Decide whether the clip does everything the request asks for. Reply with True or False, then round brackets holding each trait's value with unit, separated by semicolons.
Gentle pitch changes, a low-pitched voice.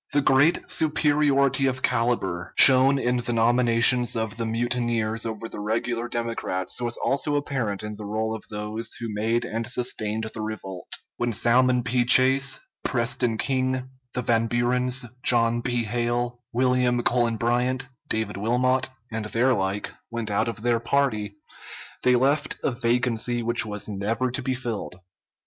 True (2.3 semitones; 120 Hz)